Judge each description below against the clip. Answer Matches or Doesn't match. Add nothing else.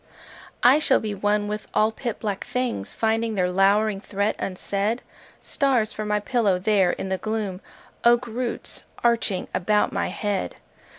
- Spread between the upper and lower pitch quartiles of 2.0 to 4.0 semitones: Matches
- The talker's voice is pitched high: Matches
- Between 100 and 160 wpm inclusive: Matches